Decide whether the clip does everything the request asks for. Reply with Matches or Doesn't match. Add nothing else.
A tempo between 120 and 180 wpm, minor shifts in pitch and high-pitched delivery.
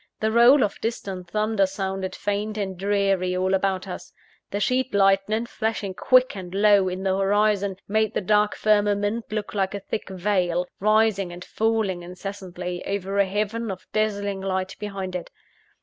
Matches